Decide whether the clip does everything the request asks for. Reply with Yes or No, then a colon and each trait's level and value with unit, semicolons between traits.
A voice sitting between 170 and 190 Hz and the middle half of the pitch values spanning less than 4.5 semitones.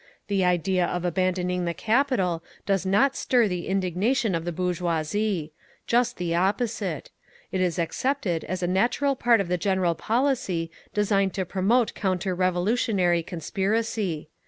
Yes: medium, 185 Hz; average, 3.6 semitones